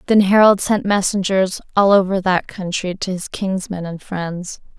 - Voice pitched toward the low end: No, high, 190 Hz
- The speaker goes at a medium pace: Yes, average, 165 wpm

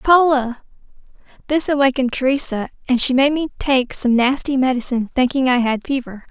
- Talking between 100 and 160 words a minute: Yes, average, 150 wpm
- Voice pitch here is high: Yes, very high, 260 Hz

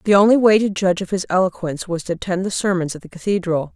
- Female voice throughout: Yes, female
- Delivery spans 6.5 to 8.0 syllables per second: Yes, 6.9 syllables/s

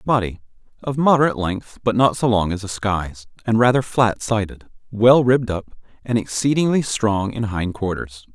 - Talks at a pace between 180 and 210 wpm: No, average, 165 wpm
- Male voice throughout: Yes, male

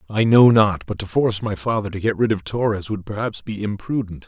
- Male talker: Yes, male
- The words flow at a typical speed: No, fast, 225 wpm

